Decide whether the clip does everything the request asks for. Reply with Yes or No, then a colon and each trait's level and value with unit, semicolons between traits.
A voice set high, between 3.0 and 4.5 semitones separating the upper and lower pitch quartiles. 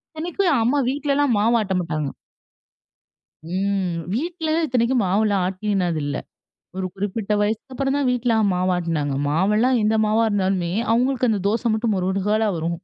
No: high, 210 Hz; average, 4.9 semitones